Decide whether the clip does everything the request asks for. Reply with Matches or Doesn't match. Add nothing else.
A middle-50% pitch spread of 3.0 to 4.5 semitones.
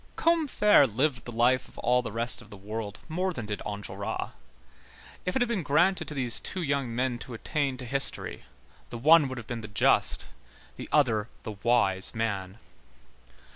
Doesn't match